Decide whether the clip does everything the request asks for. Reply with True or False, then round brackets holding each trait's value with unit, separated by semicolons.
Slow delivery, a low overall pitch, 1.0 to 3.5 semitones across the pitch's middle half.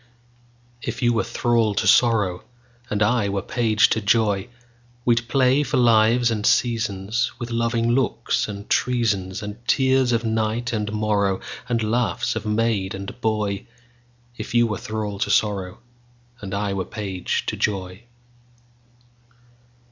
True (120 wpm; 115 Hz; 2.6 semitones)